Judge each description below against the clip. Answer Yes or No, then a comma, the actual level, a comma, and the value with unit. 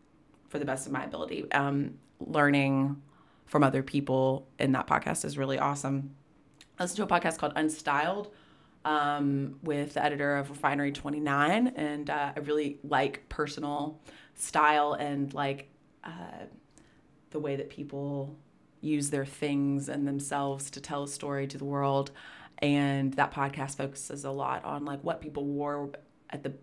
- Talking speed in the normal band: Yes, average, 160 wpm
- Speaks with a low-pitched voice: No, medium, 145 Hz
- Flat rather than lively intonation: Yes, narrow, 1.2 semitones